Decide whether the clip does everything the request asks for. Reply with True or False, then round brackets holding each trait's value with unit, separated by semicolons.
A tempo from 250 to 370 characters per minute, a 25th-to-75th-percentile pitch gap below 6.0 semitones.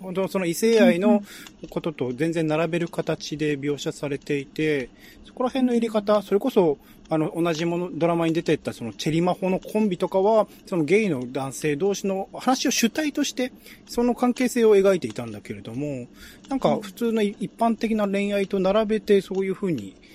True (365 characters per minute; 5.5 semitones)